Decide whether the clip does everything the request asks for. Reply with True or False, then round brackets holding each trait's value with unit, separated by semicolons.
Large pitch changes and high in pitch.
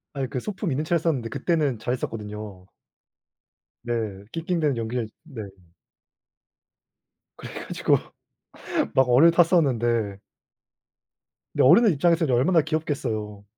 False (6.2 semitones; 130 Hz)